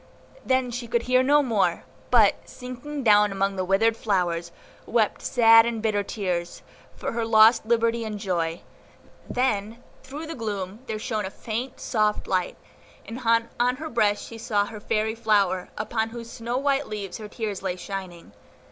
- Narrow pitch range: No, average, 3.0 semitones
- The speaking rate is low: No, average, 165 wpm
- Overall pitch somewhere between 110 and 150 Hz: No, high, 220 Hz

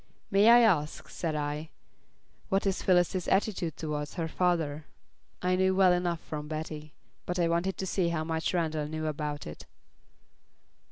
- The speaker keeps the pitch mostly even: No, average, 3.1 semitones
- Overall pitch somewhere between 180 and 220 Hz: No, medium, 165 Hz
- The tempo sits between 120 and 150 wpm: No, average, 160 wpm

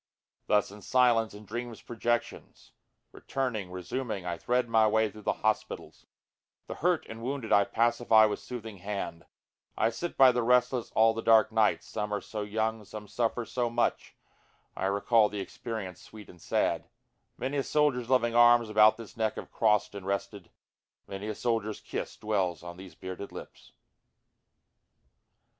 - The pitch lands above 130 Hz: No, low, 110 Hz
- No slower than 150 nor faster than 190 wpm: Yes, average, 165 wpm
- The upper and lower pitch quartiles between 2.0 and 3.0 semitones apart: Yes, narrow, 2.6 semitones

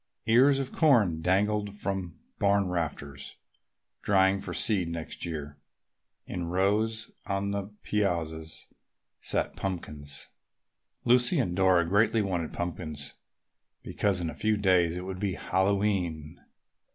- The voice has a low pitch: Yes, very low, 95 Hz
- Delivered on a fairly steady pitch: No, average, 3.6 semitones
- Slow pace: Yes, slow, 120 wpm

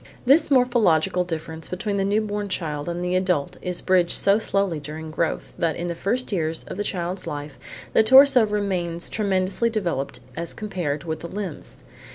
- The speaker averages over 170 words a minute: Yes, average, 185 wpm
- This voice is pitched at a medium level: Yes, medium, 180 Hz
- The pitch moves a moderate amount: Yes, average, 4.0 semitones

